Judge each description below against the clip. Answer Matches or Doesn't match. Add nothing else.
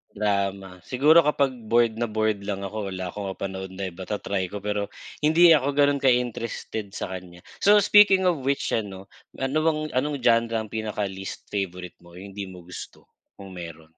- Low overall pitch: Matches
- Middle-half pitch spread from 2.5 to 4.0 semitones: Doesn't match